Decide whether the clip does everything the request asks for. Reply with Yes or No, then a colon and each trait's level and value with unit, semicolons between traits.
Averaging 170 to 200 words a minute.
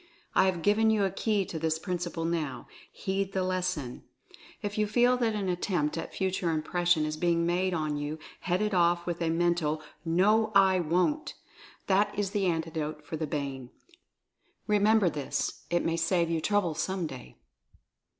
Yes: average, 180 wpm